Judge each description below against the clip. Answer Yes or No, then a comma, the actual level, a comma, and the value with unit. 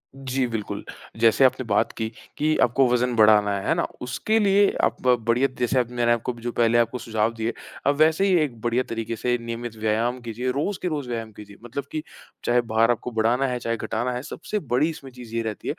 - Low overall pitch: Yes, low, 120 Hz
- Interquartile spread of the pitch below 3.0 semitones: Yes, narrow, 2.4 semitones